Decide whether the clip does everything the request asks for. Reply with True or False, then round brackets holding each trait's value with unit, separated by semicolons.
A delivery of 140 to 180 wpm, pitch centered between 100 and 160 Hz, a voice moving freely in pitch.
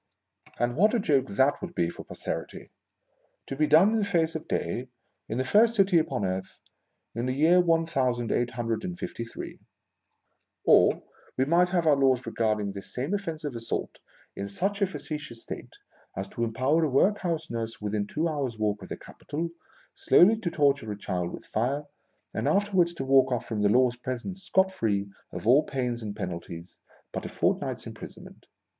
False (190 wpm; 135 Hz; 6.8 semitones)